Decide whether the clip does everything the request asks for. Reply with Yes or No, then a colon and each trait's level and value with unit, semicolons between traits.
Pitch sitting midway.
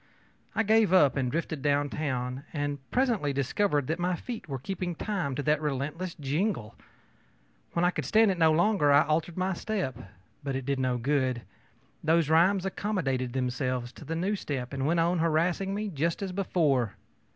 Yes: medium, 155 Hz